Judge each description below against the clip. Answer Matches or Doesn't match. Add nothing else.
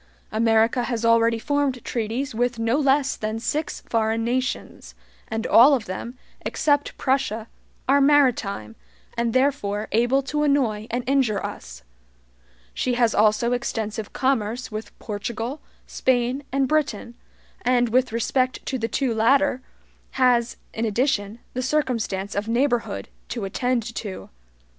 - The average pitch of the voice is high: Matches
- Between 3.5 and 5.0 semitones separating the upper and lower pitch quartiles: Doesn't match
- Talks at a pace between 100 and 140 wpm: Matches